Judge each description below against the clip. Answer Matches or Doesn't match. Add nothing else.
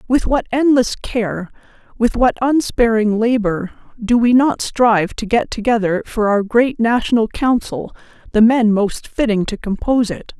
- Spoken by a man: Doesn't match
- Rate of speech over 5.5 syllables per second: Doesn't match